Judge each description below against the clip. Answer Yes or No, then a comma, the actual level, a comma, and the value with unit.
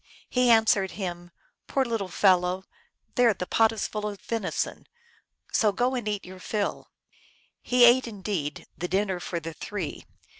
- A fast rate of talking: No, average, 160 wpm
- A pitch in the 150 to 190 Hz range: No, high, 205 Hz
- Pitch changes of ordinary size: Yes, average, 3.8 semitones